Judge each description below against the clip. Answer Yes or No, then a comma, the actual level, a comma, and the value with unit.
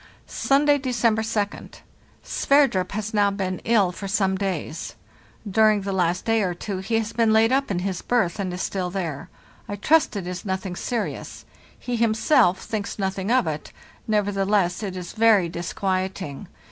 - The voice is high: Yes, high, 200 Hz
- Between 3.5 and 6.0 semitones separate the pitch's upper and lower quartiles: No, average, 3.0 semitones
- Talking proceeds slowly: No, average, 165 wpm